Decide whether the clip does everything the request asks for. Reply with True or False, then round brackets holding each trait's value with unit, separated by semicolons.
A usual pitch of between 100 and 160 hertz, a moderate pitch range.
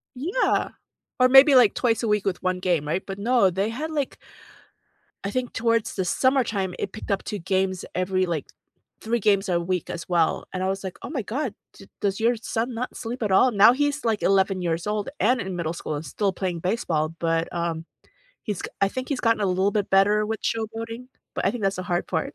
False (200 Hz; 4.0 semitones)